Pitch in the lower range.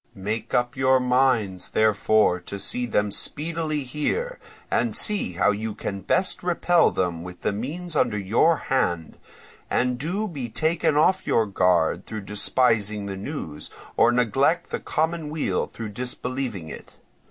Yes: low, 125 Hz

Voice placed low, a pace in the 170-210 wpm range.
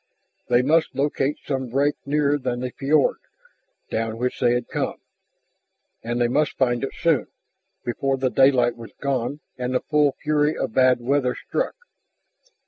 No: low, 130 Hz; average, 155 wpm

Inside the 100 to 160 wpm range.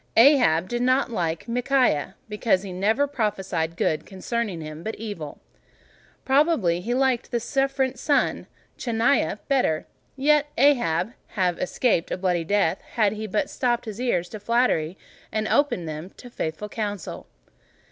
Yes: average, 150 wpm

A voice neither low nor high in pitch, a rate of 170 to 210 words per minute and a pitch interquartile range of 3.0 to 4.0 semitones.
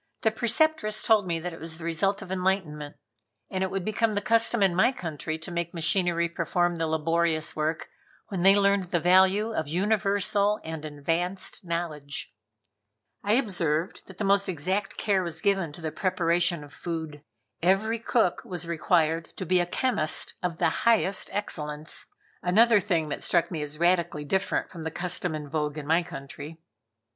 Yes: medium, 175 Hz; average, 175 wpm; average, 3.6 semitones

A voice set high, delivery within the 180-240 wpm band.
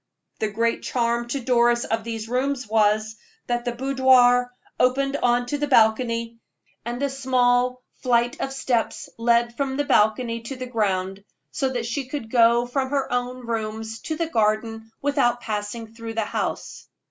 No: high, 240 Hz; average, 165 wpm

